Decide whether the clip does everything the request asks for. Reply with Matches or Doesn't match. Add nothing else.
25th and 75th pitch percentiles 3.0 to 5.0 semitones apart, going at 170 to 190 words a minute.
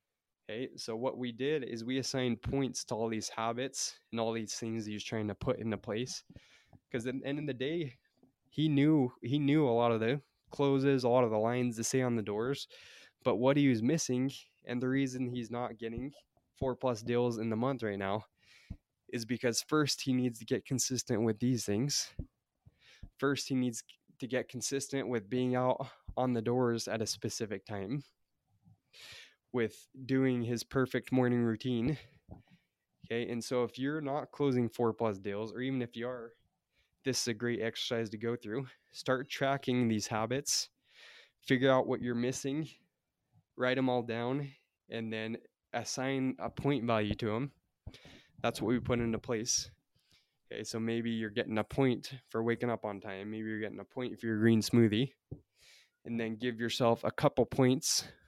Doesn't match